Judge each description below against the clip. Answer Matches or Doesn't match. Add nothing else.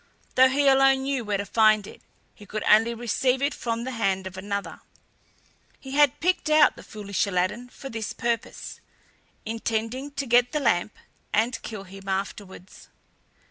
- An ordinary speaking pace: Matches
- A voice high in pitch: Matches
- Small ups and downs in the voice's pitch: Doesn't match